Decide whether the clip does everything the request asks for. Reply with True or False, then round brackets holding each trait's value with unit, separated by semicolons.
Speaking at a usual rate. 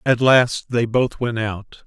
True (195 wpm)